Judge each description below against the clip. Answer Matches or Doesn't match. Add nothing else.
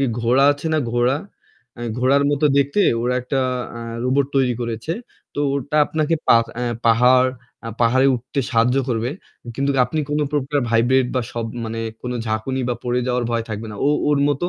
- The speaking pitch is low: Matches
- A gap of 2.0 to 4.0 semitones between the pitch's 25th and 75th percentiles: Matches